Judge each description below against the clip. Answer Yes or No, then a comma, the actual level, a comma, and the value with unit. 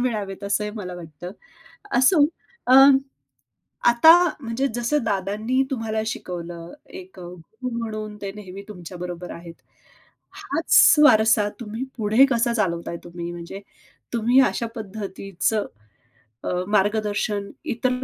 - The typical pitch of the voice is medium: No, high, 210 Hz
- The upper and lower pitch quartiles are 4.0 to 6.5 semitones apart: Yes, average, 4.3 semitones